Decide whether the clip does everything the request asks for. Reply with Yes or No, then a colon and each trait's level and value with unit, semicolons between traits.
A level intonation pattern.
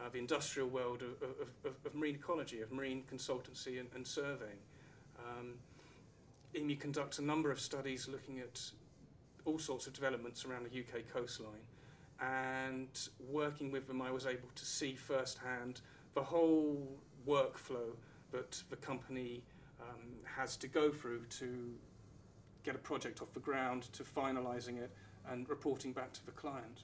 Yes: narrow, 2.3 semitones